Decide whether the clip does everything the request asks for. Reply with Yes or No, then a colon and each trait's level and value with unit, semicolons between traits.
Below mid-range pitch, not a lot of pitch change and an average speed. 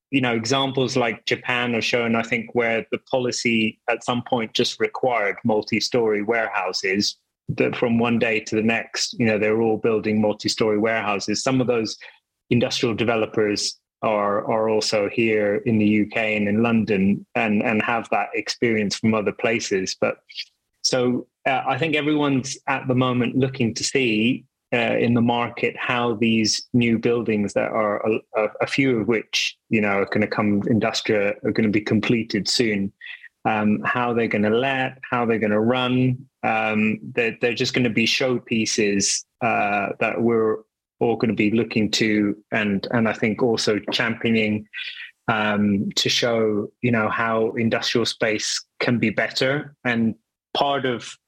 Yes: low, 115 Hz; narrow, 2.3 semitones; average, 170 wpm